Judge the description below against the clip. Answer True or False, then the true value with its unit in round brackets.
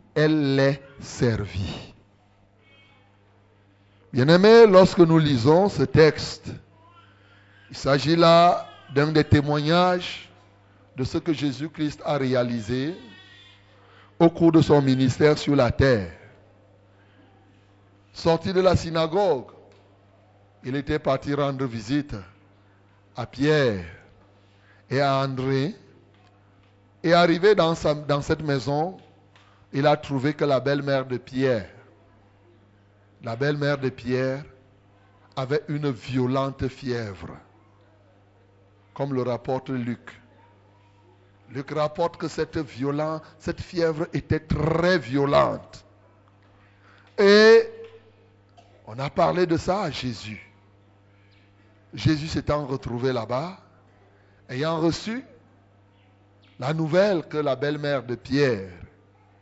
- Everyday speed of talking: False (100 wpm)